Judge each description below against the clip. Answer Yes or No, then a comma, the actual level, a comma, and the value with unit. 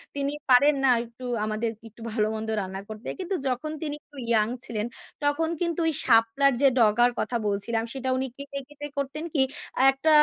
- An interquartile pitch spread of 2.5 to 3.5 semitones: No, average, 4.4 semitones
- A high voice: Yes, very high, 260 Hz